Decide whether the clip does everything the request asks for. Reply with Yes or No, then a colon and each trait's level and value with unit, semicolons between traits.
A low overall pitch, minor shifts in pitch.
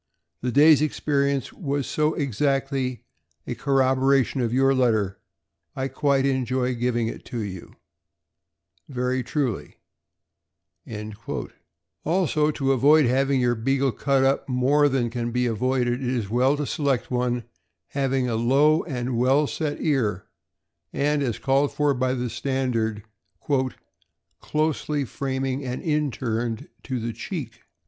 Yes: low, 130 Hz; narrow, 2.3 semitones